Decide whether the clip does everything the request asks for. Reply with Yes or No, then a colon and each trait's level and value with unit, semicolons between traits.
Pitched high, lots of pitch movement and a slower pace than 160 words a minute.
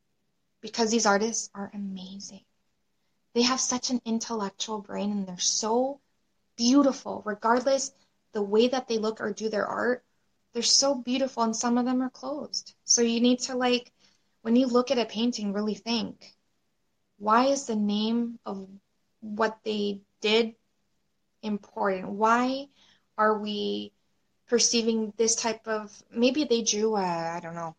No: high, 225 Hz; average, 2.9 semitones; average, 150 wpm